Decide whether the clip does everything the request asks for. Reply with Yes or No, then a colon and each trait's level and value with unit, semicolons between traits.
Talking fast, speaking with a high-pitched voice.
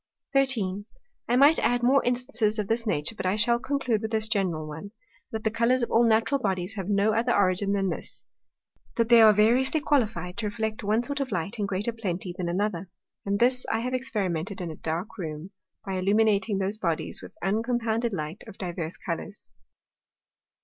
No: average, 190 wpm; high, 215 Hz